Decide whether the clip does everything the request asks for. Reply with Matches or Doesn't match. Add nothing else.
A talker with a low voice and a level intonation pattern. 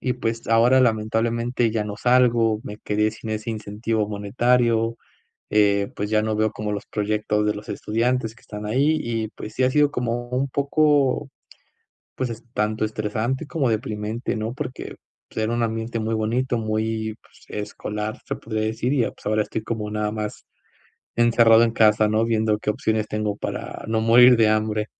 Matches